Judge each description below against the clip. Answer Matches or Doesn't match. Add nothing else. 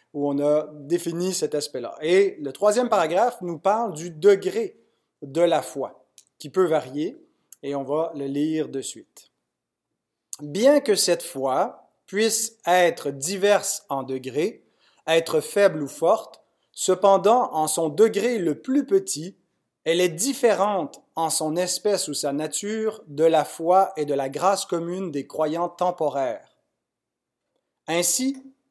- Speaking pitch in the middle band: Matches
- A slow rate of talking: Matches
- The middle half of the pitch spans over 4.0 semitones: Matches